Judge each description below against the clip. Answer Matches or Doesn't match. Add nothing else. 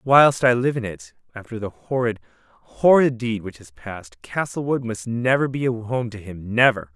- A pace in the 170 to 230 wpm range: Matches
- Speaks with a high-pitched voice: Doesn't match